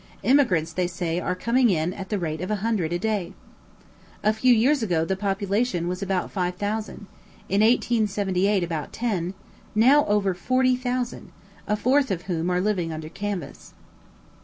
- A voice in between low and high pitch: No, high, 195 Hz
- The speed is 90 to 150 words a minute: No, average, 165 wpm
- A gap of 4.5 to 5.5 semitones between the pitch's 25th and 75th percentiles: No, average, 3.9 semitones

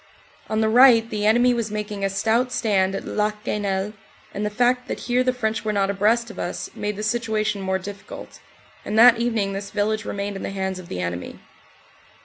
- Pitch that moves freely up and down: No, narrow, 2.6 semitones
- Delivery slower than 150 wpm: No, fast, 205 wpm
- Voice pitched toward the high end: Yes, high, 210 Hz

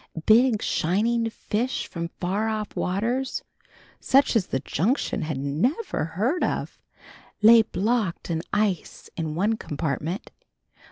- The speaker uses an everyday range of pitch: No, wide, 5.7 semitones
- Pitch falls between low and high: No, high, 210 Hz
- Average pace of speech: No, slow, 120 wpm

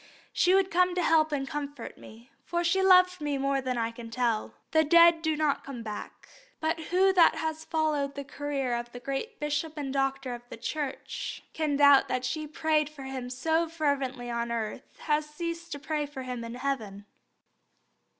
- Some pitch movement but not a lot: Yes, average, 3.8 semitones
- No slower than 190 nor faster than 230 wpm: Yes, average, 195 wpm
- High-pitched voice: Yes, very high, 290 Hz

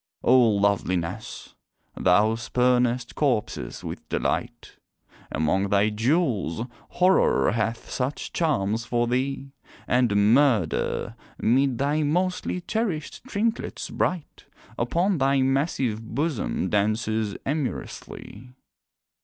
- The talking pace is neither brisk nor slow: No, slow, 95 wpm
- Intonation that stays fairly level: No, average, 5.2 semitones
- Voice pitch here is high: No, low, 125 Hz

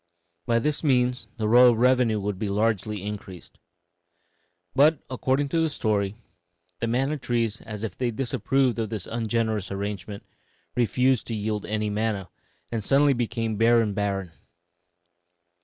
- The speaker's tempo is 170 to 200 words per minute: No, average, 140 wpm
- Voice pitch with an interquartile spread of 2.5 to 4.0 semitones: Yes, average, 3.2 semitones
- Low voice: Yes, low, 115 Hz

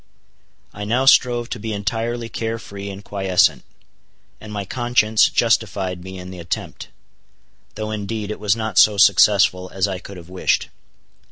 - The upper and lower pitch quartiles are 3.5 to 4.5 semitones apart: No, average, 2.9 semitones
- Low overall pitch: Yes, low, 105 Hz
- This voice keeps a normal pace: Yes, average, 160 wpm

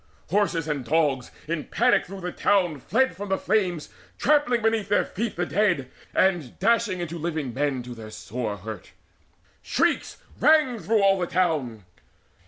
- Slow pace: No, average, 160 wpm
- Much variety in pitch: Yes, wide, 6.9 semitones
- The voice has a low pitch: No, medium, 175 Hz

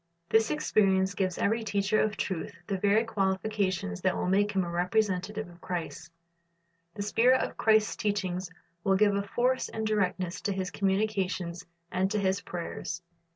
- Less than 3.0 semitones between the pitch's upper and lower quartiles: Yes, narrow, 2.6 semitones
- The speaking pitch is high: Yes, high, 195 Hz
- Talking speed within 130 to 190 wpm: Yes, average, 160 wpm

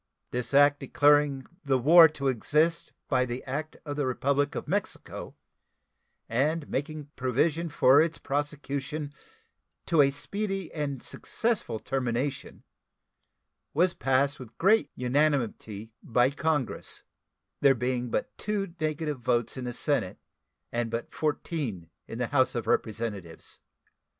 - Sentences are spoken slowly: Yes, slow, 125 wpm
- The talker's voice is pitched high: No, medium, 140 Hz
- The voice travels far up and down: No, average, 3.6 semitones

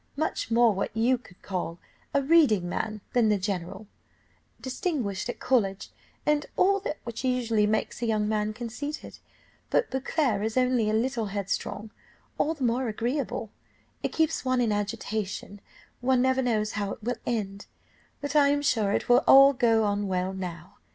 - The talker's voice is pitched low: No, high, 230 Hz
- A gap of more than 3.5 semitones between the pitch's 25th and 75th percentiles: Yes, average, 4.0 semitones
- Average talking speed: Yes, average, 170 wpm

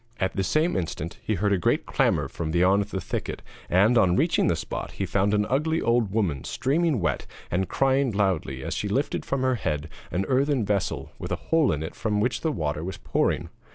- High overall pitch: No, low, 100 Hz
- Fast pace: Yes, fast, 215 wpm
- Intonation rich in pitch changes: Yes, wide, 6.7 semitones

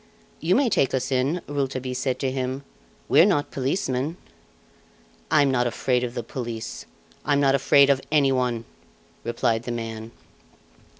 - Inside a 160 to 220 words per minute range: No, average, 145 wpm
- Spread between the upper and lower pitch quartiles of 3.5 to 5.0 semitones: No, narrow, 2.5 semitones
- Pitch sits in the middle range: No, low, 130 Hz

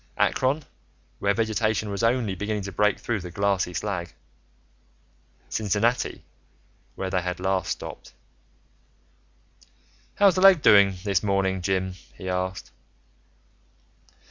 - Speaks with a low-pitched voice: Yes, low, 100 Hz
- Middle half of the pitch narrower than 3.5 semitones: Yes, average, 2.8 semitones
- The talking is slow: Yes, slow, 110 wpm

